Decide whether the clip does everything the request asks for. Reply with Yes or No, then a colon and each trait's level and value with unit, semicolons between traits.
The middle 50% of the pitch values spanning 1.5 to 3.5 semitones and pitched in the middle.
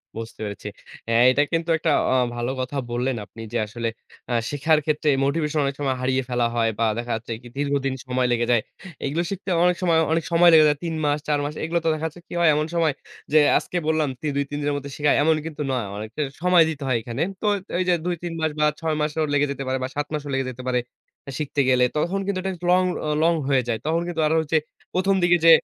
No: average, 4.1 semitones; medium, 145 Hz